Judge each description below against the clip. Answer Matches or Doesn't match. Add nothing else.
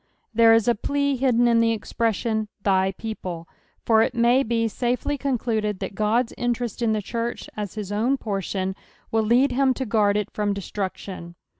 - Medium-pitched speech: Doesn't match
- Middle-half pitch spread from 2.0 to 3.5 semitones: Matches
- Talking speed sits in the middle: Matches